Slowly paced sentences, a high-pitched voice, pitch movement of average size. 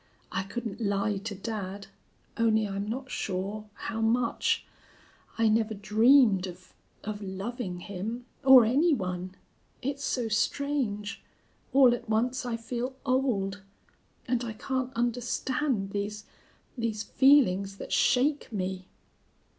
Yes: slow, 125 wpm; high, 220 Hz; average, 3.8 semitones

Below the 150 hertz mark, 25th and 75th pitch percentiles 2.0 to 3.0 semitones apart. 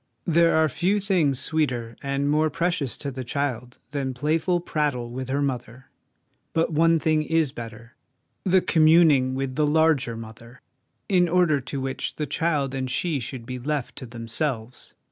No: medium, 140 Hz; average, 4.0 semitones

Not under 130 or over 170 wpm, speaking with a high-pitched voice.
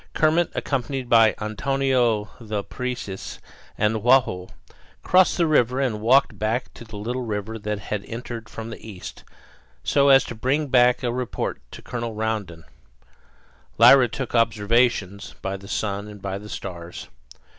No: average, 155 wpm; low, 115 Hz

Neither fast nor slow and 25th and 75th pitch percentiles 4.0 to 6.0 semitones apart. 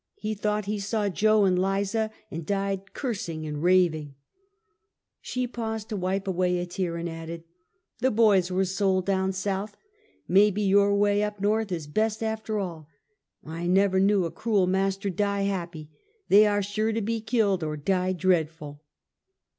No: average, 170 wpm; average, 2.8 semitones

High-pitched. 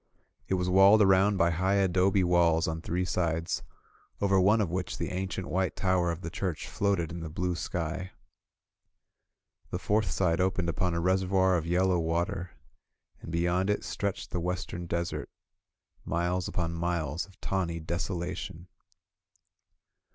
No: very low, 90 Hz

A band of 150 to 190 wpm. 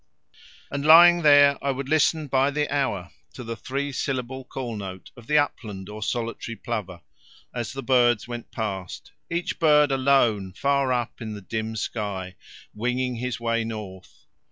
Yes: average, 170 wpm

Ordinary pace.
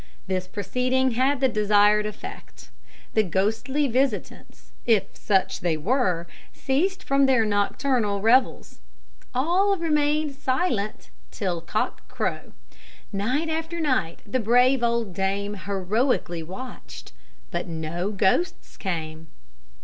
No: slow, 110 wpm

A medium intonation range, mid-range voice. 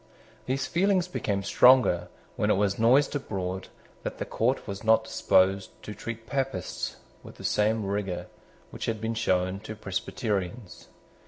No: average, 4.1 semitones; low, 110 Hz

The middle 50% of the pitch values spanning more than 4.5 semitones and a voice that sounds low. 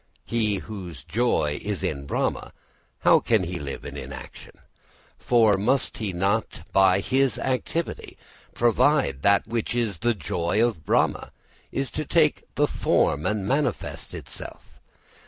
Yes: average, 5.1 semitones; low, 110 Hz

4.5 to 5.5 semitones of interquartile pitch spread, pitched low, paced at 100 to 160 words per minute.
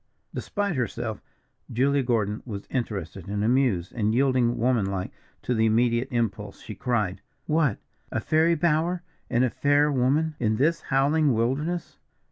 Yes: average, 4.9 semitones; low, 125 Hz; average, 140 wpm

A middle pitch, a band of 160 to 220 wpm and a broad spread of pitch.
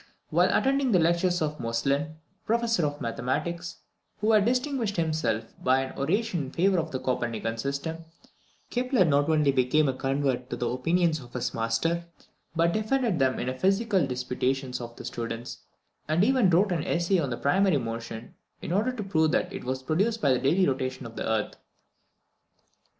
Yes: medium, 155 Hz; average, 175 wpm; wide, 6.6 semitones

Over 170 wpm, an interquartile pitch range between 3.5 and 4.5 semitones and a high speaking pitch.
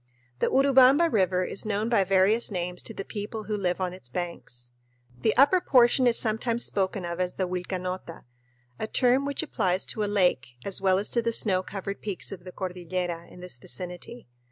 Yes: average, 195 wpm; average, 3.9 semitones; high, 195 Hz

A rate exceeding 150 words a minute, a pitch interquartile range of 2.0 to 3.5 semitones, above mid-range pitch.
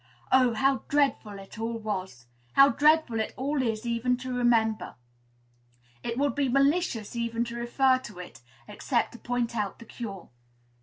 Yes: average, 160 wpm; average, 3.2 semitones; high, 235 Hz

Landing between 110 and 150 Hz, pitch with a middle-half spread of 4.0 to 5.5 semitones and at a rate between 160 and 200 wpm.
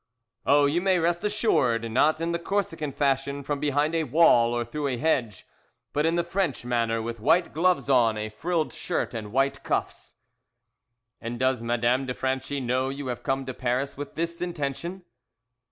Yes: medium, 140 Hz; average, 5.2 semitones; average, 180 wpm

